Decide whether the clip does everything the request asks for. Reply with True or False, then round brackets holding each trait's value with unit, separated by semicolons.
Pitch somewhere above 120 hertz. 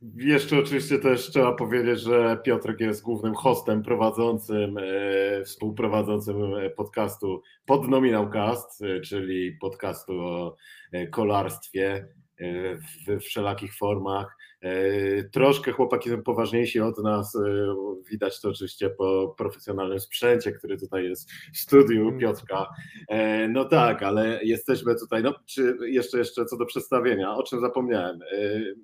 False (110 Hz)